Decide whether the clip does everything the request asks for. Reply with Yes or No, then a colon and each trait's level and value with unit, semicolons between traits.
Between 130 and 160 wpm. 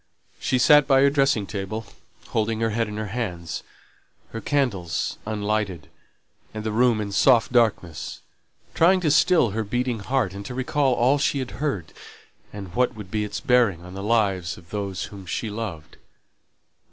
No: average, 170 wpm